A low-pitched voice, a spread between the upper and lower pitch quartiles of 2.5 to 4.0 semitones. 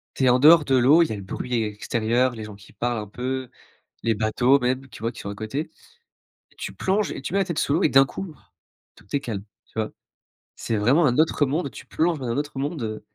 No: low, 130 Hz; average, 5.0 semitones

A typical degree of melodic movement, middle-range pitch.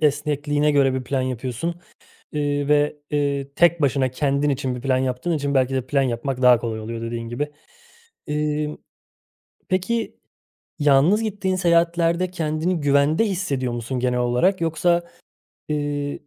Yes: average, 4.0 semitones; medium, 145 Hz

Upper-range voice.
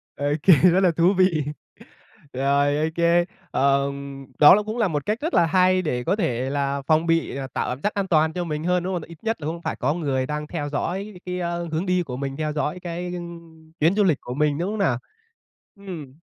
No: medium, 165 Hz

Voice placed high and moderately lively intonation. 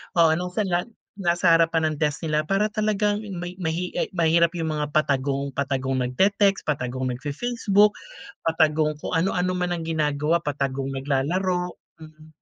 No: medium, 160 Hz; average, 3.7 semitones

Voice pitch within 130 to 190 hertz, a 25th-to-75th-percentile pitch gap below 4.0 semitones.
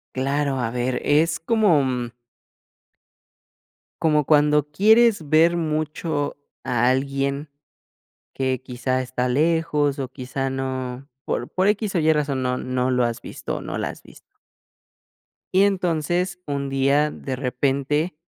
Yes: medium, 140 Hz; average, 3.5 semitones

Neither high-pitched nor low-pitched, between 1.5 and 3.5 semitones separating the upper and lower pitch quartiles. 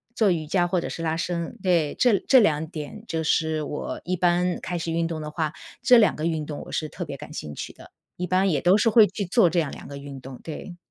Yes: medium, 165 Hz; average, 3.1 semitones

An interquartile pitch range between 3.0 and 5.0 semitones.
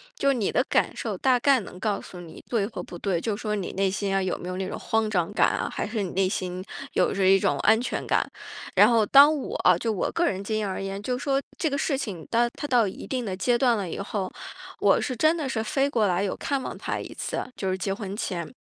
Yes: average, 4.6 semitones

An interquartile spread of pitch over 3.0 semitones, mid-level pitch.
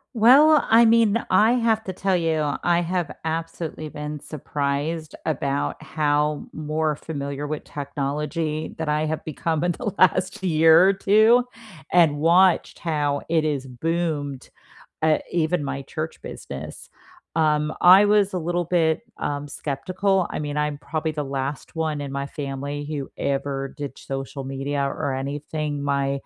Yes: average, 3.5 semitones; medium, 155 Hz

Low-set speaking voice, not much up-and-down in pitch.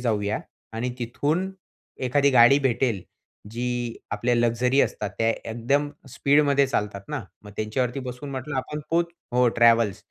No: low, 125 Hz; average, 3.3 semitones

